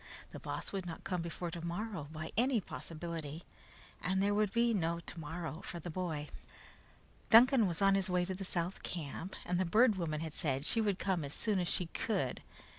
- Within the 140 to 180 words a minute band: No, average, 195 wpm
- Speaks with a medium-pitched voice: Yes, medium, 180 Hz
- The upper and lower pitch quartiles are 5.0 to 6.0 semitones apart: No, average, 3.3 semitones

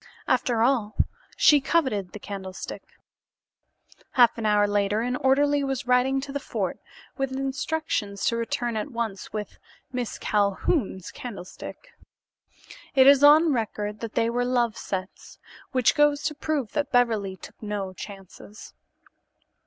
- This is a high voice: Yes, high, 235 Hz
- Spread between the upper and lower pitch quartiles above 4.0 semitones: Yes, average, 4.7 semitones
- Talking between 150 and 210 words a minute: No, slow, 135 wpm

